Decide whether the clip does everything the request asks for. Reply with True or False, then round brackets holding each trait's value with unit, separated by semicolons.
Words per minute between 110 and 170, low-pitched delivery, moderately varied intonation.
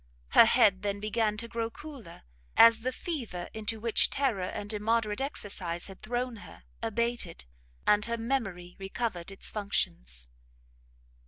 False (140 wpm; 215 Hz; 3.2 semitones)